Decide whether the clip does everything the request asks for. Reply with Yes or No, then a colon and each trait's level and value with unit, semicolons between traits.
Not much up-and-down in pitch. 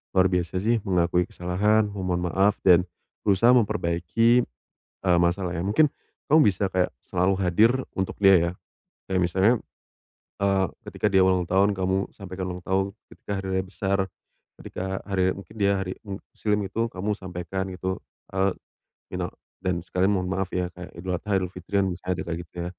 Yes: narrow, 1.6 semitones